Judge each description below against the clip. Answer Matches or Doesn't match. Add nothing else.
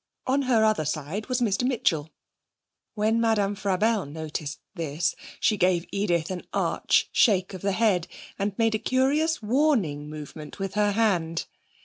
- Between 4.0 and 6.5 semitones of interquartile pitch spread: Matches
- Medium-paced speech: Matches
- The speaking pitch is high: Matches